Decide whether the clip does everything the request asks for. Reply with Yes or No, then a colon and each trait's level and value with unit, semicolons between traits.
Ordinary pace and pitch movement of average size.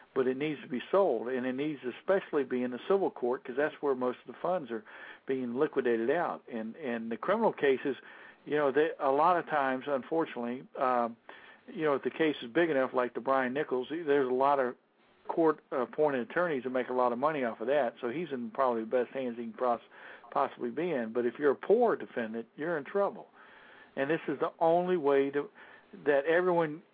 No: fast, 225 wpm; average, 3.8 semitones